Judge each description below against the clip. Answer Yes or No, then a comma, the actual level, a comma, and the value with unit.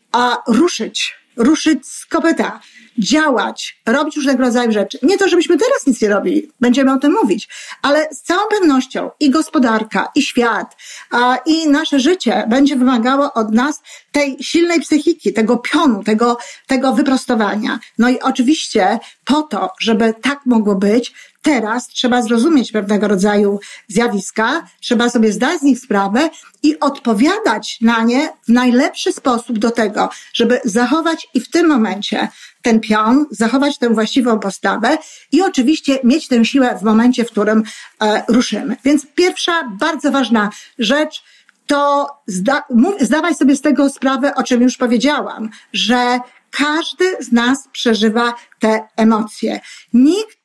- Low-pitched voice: No, very high, 255 Hz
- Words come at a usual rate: Yes, average, 145 wpm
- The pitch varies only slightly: No, average, 4.3 semitones